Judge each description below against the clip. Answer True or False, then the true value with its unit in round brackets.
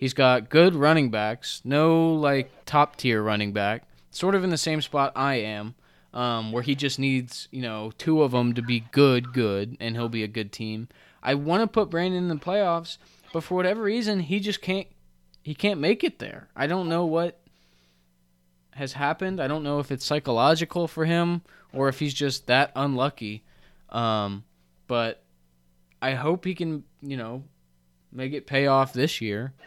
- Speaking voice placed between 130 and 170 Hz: True (135 Hz)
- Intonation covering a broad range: True (6.6 semitones)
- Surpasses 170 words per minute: True (190 wpm)